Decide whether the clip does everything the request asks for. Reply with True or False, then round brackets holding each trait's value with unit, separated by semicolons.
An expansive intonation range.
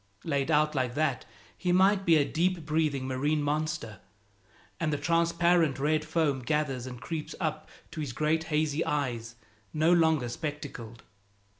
False (2.8 semitones)